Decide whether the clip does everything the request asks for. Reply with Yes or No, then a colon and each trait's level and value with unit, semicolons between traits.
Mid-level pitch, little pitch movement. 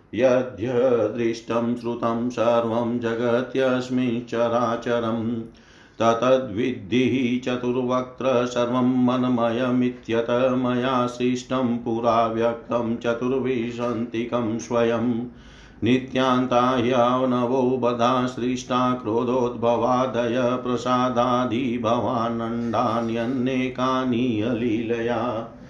No: low, 120 Hz; narrow, 1.3 semitones